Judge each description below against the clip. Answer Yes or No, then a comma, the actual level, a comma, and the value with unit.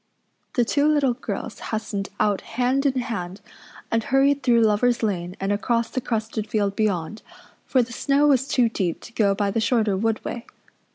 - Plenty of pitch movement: No, average, 3.6 semitones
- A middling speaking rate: Yes, average, 180 wpm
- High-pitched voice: Yes, high, 225 Hz